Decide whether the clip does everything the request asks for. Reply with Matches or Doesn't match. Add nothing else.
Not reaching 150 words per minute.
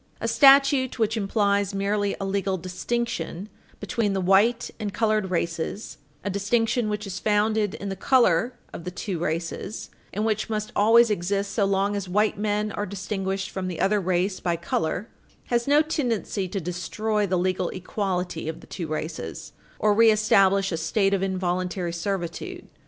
Doesn't match